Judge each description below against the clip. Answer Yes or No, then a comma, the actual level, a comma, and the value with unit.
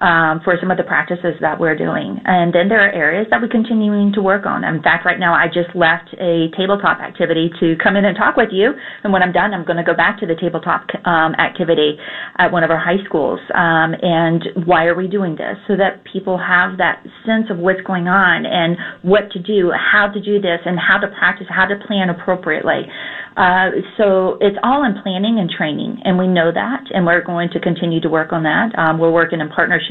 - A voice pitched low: No, medium, 180 Hz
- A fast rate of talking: Yes, fast, 235 wpm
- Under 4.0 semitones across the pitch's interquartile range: Yes, average, 3.1 semitones